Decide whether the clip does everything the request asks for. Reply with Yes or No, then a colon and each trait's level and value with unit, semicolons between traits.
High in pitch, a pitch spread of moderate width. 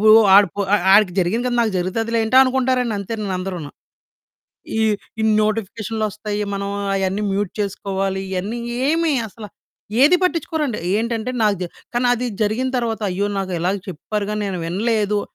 Yes: high, 210 Hz; average, 3.1 semitones